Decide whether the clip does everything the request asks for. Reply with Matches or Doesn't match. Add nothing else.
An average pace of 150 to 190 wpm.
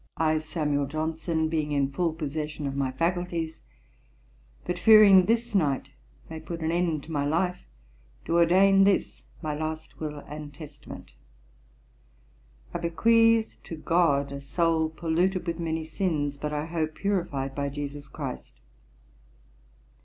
Doesn't match